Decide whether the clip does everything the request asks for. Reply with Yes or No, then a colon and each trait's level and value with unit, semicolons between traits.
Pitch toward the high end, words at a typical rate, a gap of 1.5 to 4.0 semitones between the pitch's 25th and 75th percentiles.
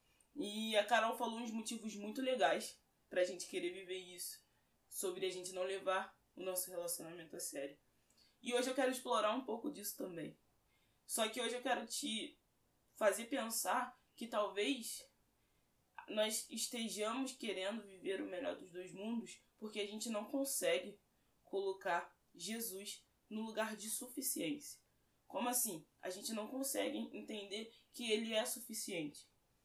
No: high, 220 Hz; average, 150 wpm; average, 4.5 semitones